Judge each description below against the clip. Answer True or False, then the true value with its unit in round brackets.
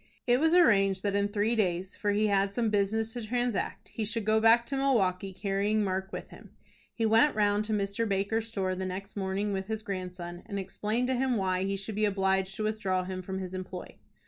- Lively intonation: False (2.5 semitones)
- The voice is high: True (205 Hz)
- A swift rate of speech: True (220 wpm)